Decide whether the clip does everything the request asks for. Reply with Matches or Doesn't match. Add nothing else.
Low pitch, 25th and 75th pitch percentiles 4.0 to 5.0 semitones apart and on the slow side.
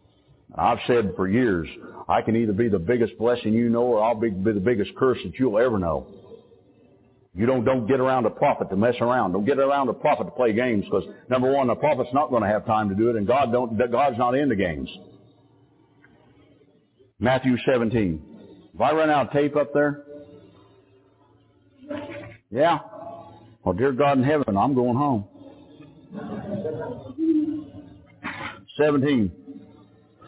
Doesn't match